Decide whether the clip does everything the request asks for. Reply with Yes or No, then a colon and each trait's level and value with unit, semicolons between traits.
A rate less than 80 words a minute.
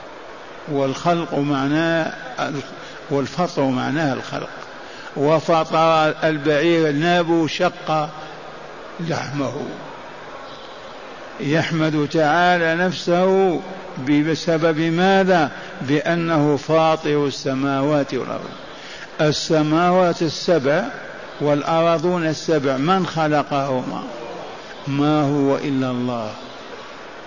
Yes: slow, 65 wpm